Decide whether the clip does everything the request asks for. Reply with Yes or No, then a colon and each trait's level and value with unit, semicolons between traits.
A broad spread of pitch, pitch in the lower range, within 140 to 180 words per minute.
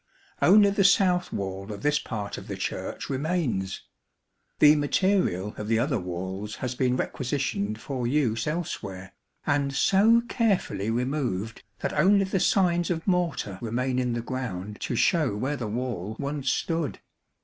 Yes: wide, 7.8 semitones; low, 130 Hz; average, 150 wpm